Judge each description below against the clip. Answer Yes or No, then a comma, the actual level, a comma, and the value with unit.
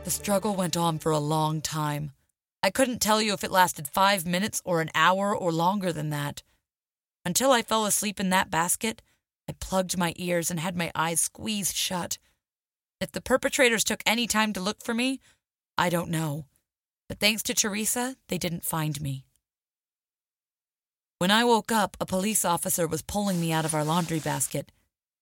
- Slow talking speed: No, average, 185 wpm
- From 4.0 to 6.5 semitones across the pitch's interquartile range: Yes, average, 4.8 semitones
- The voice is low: No, medium, 180 Hz